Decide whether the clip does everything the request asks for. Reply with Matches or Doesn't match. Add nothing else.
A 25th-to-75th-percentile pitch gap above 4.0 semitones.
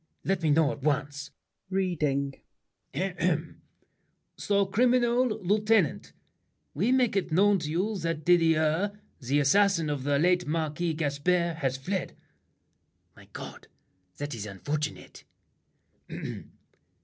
Matches